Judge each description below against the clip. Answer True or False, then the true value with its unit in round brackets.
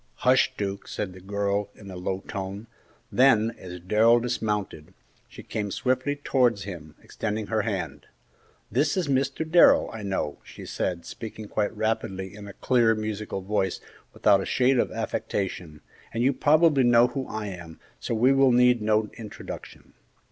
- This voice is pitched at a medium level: False (110 Hz)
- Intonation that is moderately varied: True (4.1 semitones)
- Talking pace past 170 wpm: False (160 wpm)